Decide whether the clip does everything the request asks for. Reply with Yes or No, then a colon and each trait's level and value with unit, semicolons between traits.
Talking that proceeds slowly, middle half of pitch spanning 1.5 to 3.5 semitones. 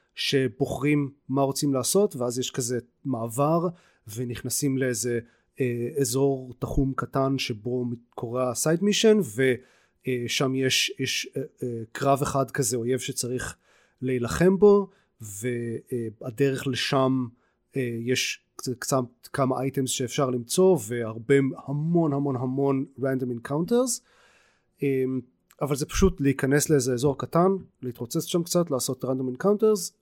No: average, 120 wpm; average, 2.7 semitones